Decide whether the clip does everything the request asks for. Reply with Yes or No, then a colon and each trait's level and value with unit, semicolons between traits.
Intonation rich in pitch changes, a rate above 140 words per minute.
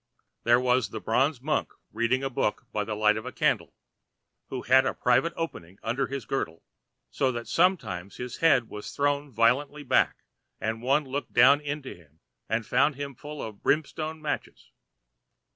No: average, 4.2 semitones; average, 170 wpm